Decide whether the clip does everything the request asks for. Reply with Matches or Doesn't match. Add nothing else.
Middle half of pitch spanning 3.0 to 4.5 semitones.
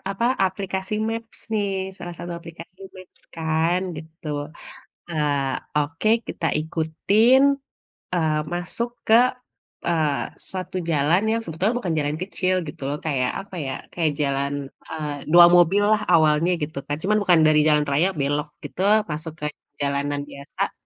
Matches